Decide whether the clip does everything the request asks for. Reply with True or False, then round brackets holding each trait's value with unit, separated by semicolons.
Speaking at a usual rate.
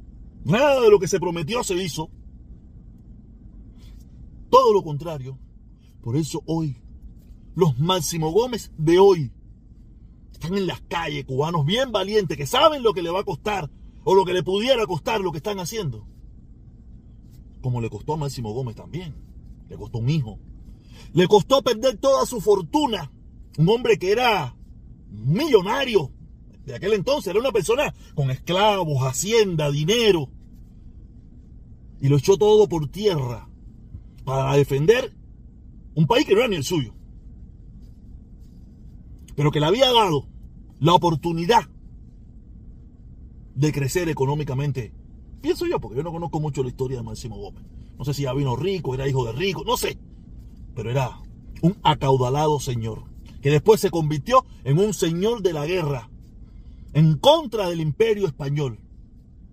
True (145 wpm)